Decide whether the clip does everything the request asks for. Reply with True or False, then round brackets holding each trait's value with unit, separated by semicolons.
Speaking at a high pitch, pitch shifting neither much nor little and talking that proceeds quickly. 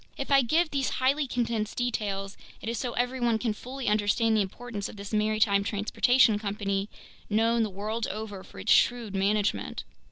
False (220 Hz; 3.0 semitones; 170 wpm)